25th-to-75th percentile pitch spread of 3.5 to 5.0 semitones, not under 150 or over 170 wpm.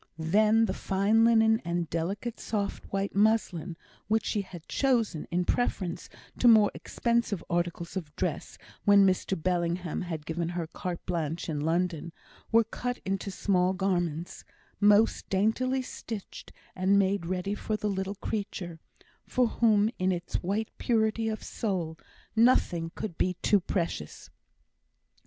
No: average, 4.0 semitones; average, 140 wpm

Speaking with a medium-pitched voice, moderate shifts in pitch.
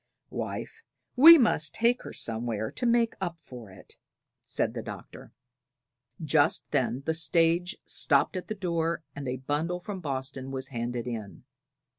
No: medium, 155 Hz; wide, 5.7 semitones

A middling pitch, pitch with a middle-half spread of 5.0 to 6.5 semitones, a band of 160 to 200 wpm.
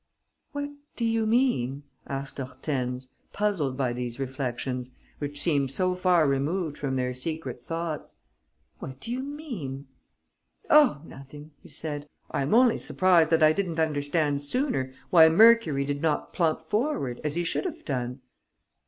No: medium, 150 Hz; wide, 5.4 semitones; average, 150 wpm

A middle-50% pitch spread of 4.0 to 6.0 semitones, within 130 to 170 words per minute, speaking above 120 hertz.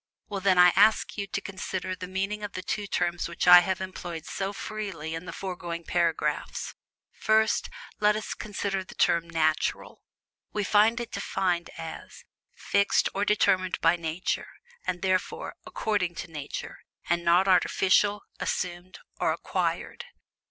No: average, 2.8 semitones; average, 150 wpm; medium, 185 Hz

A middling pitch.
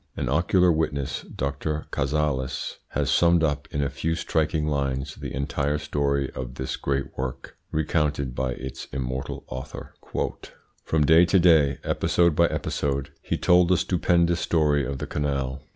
No: very low, 75 Hz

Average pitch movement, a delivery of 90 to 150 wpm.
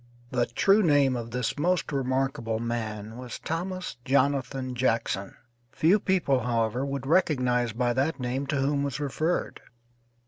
Yes: average, 3.3 semitones; average, 140 wpm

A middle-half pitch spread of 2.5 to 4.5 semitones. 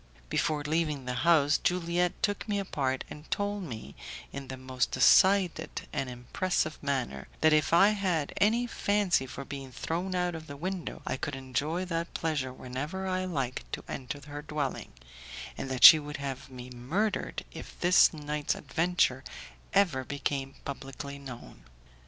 No: average, 5.0 semitones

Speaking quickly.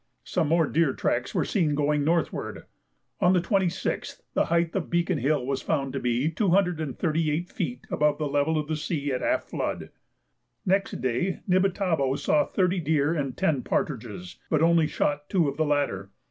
No: average, 175 wpm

